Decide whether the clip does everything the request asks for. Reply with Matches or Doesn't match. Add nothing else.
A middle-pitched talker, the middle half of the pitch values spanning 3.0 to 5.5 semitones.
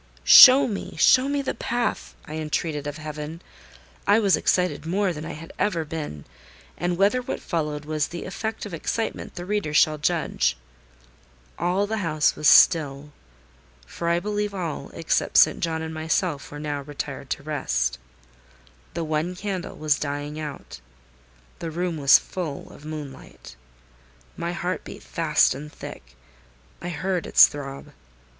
Matches